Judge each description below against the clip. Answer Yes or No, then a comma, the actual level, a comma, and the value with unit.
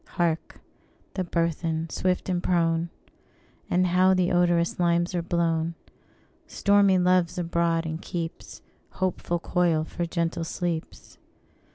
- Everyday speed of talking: No, slow, 120 wpm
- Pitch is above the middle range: No, medium, 170 Hz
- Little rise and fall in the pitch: Yes, narrow, 1.3 semitones